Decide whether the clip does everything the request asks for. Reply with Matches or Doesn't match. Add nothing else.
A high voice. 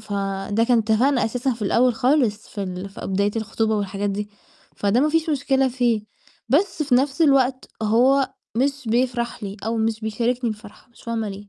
Matches